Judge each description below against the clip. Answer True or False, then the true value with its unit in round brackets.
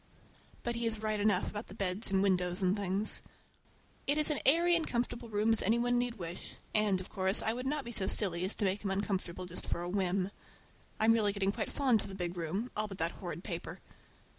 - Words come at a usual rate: False (240 wpm)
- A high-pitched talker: True (205 Hz)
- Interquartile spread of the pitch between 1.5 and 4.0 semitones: True (3.6 semitones)